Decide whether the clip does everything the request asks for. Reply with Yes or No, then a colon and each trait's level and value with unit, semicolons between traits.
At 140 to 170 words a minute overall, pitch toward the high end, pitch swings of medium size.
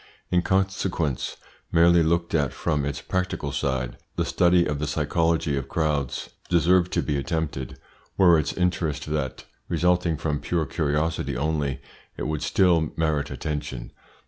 No: average, 145 wpm; very low, 80 Hz; average, 3.0 semitones